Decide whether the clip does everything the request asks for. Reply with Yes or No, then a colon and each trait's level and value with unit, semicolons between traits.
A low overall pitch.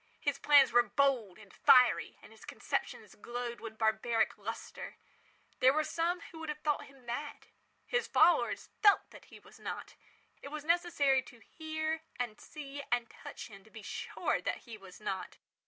No: very high, 260 Hz